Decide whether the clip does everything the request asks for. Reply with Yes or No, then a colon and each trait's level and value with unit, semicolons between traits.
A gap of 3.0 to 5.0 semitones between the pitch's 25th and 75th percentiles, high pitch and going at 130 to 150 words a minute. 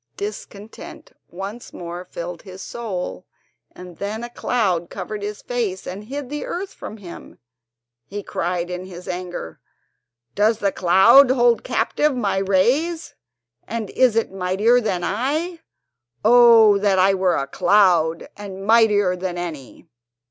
Yes: average, 4.2 semitones; high, 200 Hz; average, 140 wpm